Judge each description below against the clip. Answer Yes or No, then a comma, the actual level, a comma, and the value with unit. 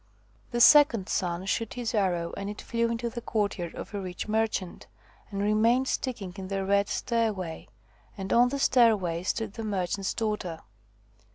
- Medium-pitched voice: No, high, 210 Hz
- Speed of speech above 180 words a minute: No, average, 165 wpm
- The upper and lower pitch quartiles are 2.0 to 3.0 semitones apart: No, average, 3.5 semitones